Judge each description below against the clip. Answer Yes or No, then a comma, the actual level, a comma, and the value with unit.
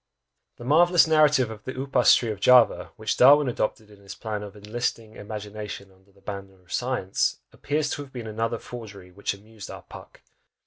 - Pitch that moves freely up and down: No, average, 3.9 semitones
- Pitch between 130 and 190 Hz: No, low, 110 Hz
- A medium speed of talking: Yes, average, 185 wpm